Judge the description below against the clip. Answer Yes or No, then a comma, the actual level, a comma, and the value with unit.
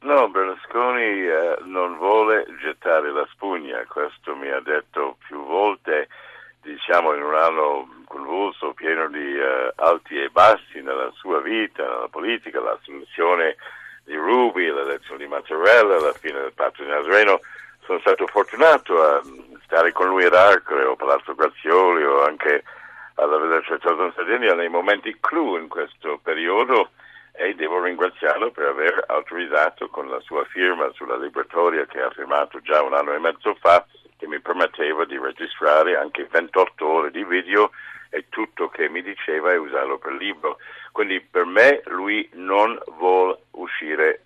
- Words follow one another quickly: No, average, 155 wpm